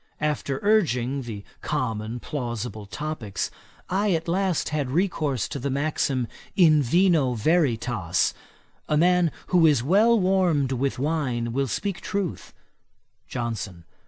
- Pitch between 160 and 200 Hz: No, medium, 140 Hz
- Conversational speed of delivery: No, slow, 125 wpm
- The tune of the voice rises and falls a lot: Yes, wide, 6.3 semitones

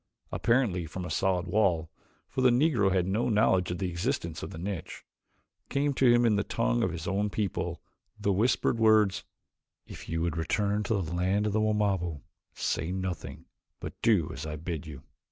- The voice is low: Yes, very low, 95 Hz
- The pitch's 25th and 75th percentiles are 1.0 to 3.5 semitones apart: No, average, 4.0 semitones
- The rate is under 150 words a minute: No, average, 190 wpm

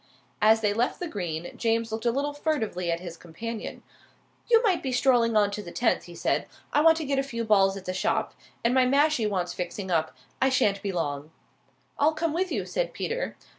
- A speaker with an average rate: No, fast, 215 wpm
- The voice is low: No, high, 225 Hz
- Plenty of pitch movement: Yes, wide, 7.0 semitones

